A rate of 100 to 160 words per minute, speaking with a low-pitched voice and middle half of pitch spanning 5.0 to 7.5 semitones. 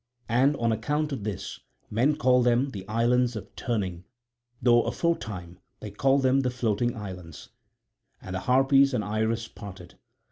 No: average, 150 wpm; low, 115 Hz; average, 4.1 semitones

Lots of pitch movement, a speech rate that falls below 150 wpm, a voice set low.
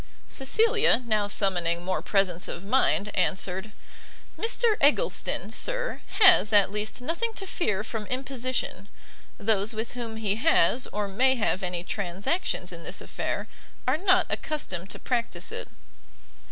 No: wide, 6.4 semitones; average, 140 wpm; high, 220 Hz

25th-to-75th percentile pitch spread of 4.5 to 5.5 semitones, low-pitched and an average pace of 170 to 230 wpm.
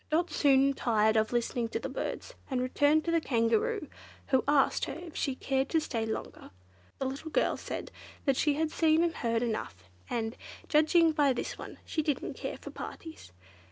No: average, 5.0 semitones; very high, 275 Hz; average, 185 wpm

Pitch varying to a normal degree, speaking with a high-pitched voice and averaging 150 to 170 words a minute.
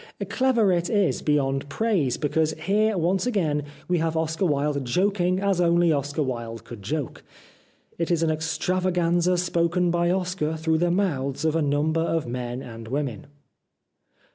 No: average, 3.8 semitones; medium, 165 Hz; average, 155 wpm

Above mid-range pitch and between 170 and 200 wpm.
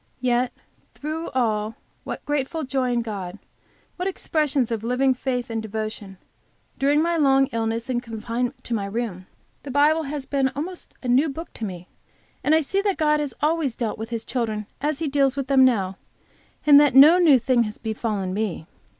Yes: very high, 255 Hz; average, 190 wpm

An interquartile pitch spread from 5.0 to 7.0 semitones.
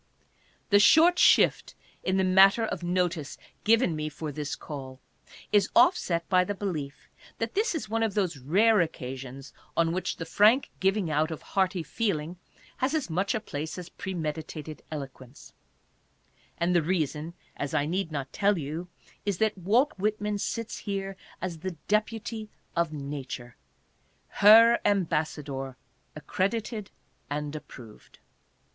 Yes: wide, 5.5 semitones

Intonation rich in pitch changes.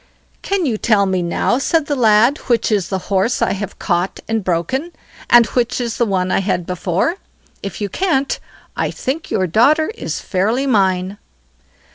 Yes: wide, 5.7 semitones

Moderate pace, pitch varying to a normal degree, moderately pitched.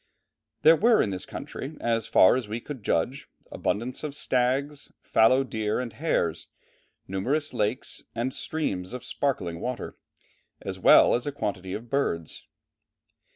No: average, 145 wpm; average, 5.0 semitones; low, 125 Hz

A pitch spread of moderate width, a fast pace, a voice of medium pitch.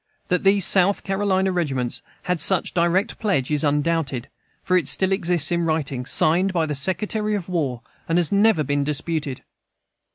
No: average, 4.5 semitones; average, 165 wpm; medium, 170 Hz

